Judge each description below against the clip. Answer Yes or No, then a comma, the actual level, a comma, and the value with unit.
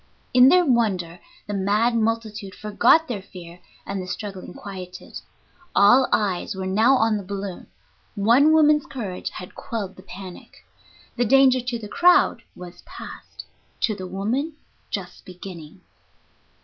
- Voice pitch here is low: No, high, 205 Hz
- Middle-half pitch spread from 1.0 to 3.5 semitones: No, average, 4.5 semitones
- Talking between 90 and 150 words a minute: Yes, average, 140 wpm